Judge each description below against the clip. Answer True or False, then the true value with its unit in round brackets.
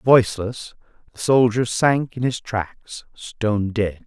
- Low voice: True (115 Hz)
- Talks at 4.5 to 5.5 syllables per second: False (3.6 syllables/s)